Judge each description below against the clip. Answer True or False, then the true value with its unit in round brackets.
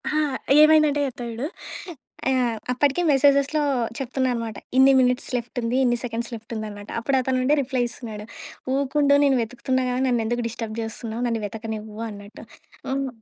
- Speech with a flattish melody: False (3.0 semitones)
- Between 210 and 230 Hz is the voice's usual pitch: False (245 Hz)